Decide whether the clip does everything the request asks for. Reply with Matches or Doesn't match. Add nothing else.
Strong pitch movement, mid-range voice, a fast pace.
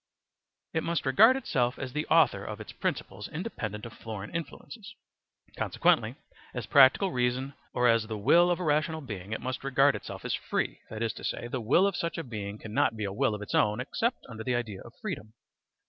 Doesn't match